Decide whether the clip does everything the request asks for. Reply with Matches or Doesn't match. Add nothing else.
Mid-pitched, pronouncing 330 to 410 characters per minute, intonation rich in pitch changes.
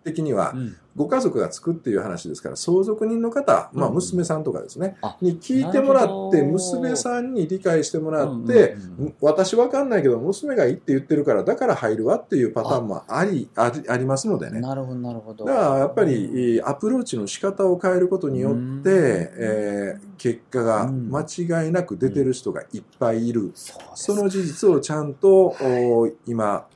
Matches